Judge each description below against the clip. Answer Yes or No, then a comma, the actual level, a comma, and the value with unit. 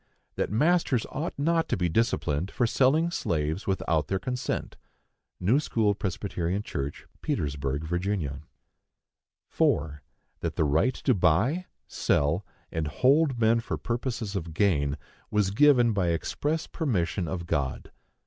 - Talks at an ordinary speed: No, slow, 130 wpm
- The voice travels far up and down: Yes, wide, 7.8 semitones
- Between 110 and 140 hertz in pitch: No, low, 100 Hz